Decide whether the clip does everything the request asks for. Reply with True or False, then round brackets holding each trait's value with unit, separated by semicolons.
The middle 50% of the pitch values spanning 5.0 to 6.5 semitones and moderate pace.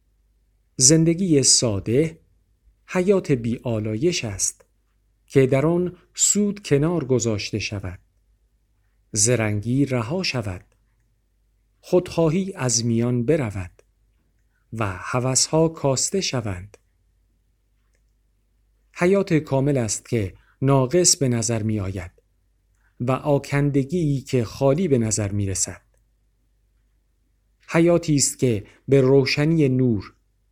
False (5.5 semitones; 90 wpm)